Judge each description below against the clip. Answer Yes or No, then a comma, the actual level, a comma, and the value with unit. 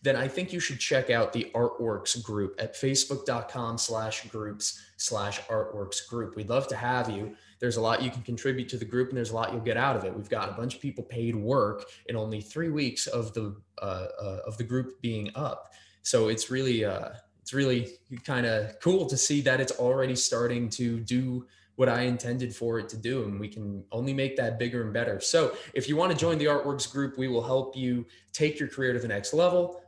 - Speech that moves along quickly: Yes, fast, 225 wpm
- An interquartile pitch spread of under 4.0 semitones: Yes, average, 2.9 semitones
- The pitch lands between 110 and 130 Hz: Yes, low, 120 Hz